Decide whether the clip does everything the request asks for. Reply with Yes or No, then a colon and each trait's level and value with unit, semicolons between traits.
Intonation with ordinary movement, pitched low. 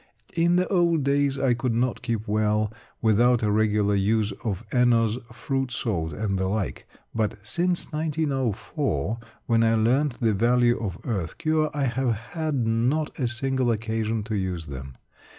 Yes: average, 4.1 semitones; low, 115 Hz